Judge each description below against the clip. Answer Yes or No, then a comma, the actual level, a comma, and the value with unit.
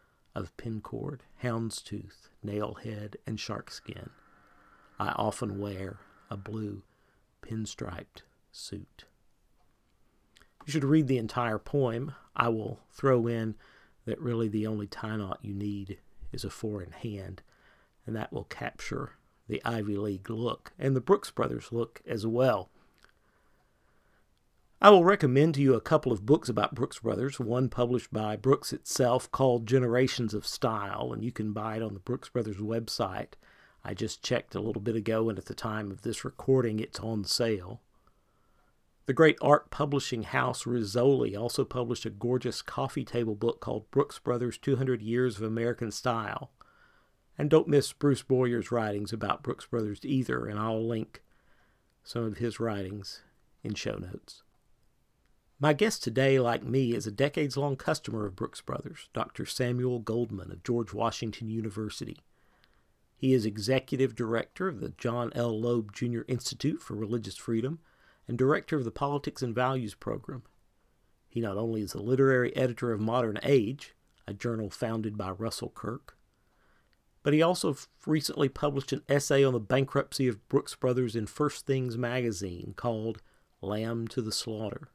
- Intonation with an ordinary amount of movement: Yes, average, 3.4 semitones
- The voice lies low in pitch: Yes, low, 120 Hz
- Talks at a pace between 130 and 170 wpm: Yes, average, 160 wpm